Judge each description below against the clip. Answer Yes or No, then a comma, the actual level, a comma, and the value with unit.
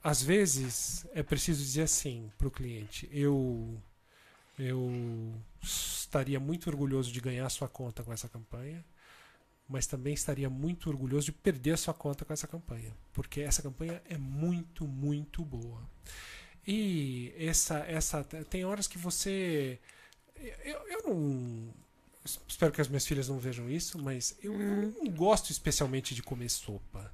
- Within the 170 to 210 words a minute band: No, average, 155 wpm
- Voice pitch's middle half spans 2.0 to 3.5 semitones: No, average, 4.3 semitones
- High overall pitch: No, medium, 145 Hz